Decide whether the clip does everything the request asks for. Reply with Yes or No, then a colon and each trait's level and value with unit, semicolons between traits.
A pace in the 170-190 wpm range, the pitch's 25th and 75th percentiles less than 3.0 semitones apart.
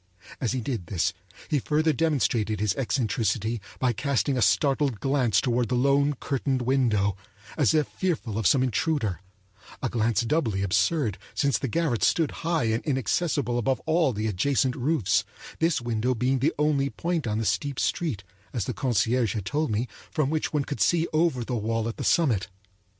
No: average, 175 wpm; average, 4.7 semitones